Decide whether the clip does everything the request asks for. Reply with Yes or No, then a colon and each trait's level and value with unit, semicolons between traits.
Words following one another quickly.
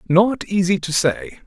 No: average, 165 wpm